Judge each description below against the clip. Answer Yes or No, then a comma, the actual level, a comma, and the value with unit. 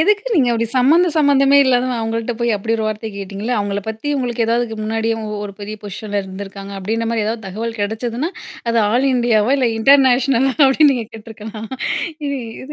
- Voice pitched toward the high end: Yes, high, 230 Hz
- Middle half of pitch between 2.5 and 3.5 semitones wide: Yes, average, 3.2 semitones